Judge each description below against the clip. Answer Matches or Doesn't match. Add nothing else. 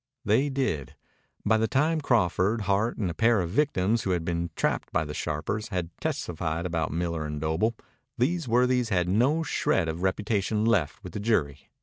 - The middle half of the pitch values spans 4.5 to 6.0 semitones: Matches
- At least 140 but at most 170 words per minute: Doesn't match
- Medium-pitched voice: Doesn't match